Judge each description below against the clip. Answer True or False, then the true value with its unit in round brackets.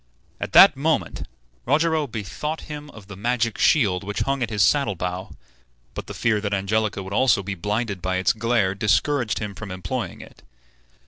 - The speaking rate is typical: True (180 wpm)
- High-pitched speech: False (105 Hz)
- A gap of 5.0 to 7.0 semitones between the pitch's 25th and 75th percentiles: False (4.0 semitones)